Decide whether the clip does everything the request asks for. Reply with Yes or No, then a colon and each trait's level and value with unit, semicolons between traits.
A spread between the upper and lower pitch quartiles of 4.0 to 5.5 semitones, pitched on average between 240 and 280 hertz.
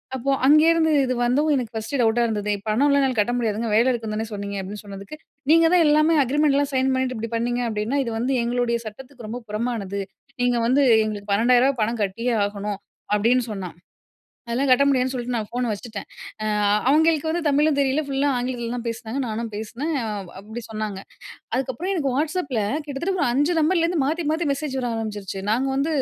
Yes: average, 4.3 semitones; high, 245 Hz